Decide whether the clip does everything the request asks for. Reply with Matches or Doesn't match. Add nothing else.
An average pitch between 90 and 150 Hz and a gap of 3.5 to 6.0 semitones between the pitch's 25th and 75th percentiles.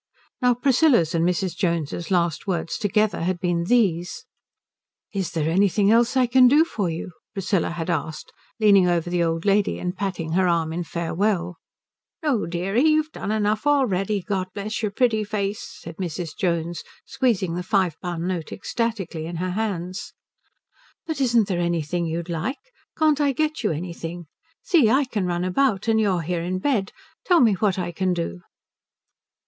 Doesn't match